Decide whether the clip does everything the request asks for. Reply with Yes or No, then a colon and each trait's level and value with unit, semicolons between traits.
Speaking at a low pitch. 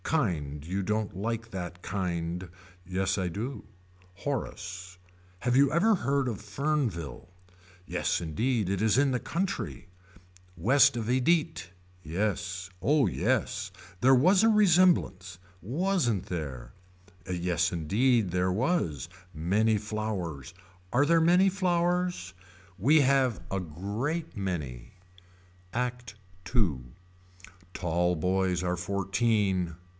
Yes: low, 105 Hz